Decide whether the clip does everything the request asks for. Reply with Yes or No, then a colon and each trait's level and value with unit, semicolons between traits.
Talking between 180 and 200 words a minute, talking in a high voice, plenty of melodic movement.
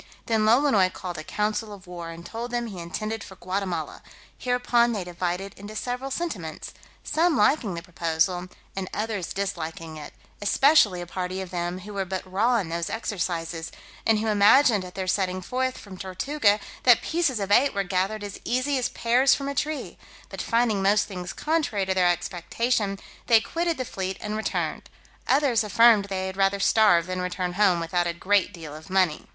No: average, 185 wpm; high, 200 Hz; average, 4.3 semitones